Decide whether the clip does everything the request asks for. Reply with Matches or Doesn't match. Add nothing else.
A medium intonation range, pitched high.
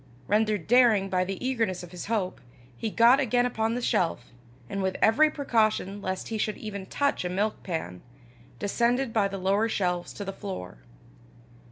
Matches